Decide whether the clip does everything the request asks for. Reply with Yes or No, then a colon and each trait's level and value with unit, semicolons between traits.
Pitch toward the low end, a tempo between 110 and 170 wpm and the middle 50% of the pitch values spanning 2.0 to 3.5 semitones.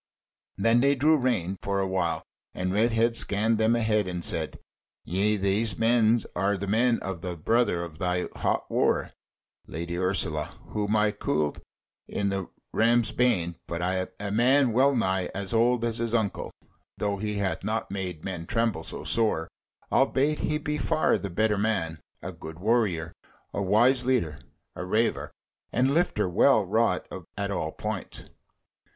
No: low, 105 Hz; average, 155 wpm; average, 4.2 semitones